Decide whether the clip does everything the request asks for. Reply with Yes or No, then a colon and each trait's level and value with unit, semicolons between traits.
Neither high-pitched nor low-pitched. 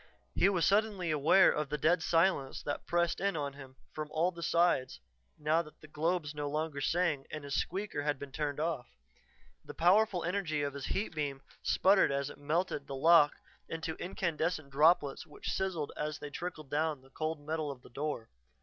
Yes: medium, 155 Hz